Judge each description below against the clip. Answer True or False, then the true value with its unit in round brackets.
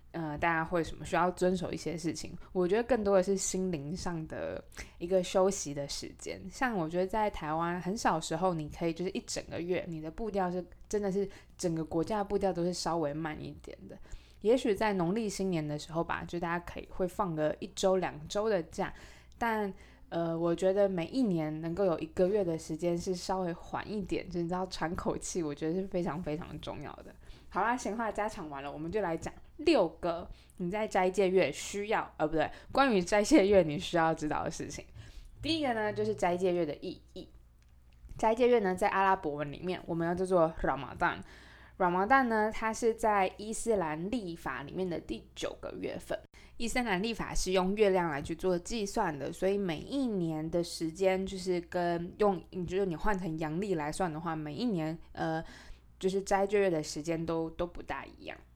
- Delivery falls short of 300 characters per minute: False (310 characters per minute)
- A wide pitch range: False (3.6 semitones)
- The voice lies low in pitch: False (180 Hz)